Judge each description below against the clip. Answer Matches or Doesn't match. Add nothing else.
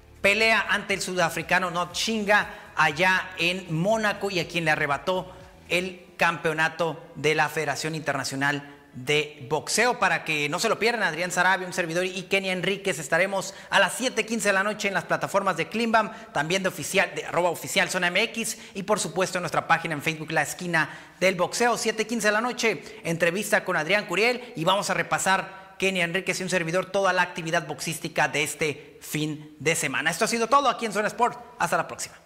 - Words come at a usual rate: Doesn't match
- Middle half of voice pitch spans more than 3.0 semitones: Matches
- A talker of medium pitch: Matches